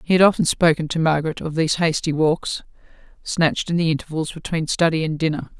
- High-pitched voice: No, medium, 160 Hz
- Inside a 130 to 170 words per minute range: No, average, 195 wpm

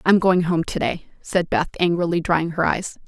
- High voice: No, medium, 170 Hz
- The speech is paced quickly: No, average, 195 wpm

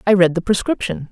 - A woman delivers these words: Yes, female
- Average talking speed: No, fast, 215 wpm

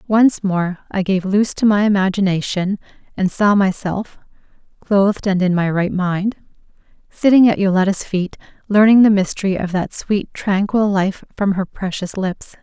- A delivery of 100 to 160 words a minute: Yes, average, 155 wpm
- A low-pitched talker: No, high, 195 Hz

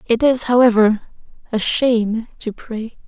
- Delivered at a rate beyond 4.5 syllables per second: No, 4.2 syllables/s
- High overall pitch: Yes, high, 230 Hz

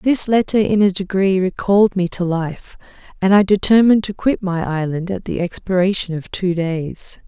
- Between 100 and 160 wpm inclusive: No, average, 180 wpm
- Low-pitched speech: No, high, 190 Hz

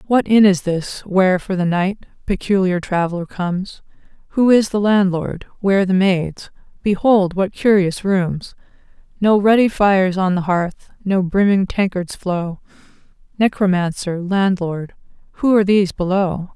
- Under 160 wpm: Yes, average, 140 wpm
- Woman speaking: Yes, female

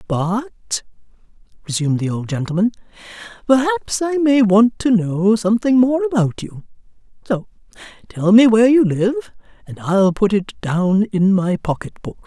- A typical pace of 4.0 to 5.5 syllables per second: Yes, 4.6 syllables/s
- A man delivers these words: No, female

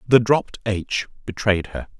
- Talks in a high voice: No, low, 105 Hz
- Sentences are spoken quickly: No, average, 150 wpm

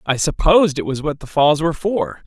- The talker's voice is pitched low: No, medium, 150 Hz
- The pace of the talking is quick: Yes, fast, 240 wpm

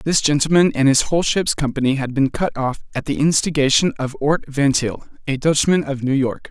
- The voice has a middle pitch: Yes, medium, 145 Hz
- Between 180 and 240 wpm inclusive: Yes, fast, 205 wpm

